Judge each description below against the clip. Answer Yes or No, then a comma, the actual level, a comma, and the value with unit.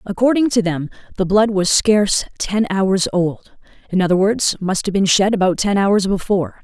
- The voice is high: Yes, high, 195 Hz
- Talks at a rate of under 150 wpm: No, average, 190 wpm